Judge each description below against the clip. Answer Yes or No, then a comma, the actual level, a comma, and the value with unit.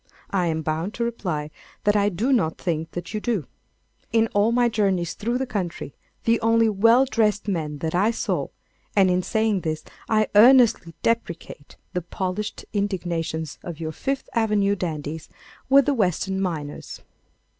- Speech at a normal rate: Yes, average, 155 wpm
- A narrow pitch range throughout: No, average, 5.2 semitones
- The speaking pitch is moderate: No, high, 200 Hz